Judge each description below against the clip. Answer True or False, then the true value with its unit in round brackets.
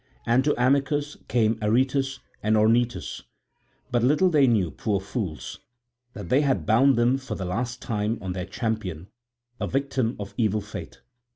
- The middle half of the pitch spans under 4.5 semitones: True (3.9 semitones)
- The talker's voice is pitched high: False (120 Hz)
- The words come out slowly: False (160 wpm)